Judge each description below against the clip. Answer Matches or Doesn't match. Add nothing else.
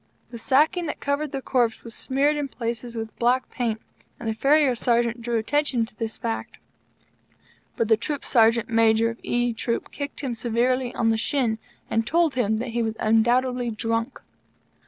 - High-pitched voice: Matches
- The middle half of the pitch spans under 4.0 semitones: Matches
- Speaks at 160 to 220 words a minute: Matches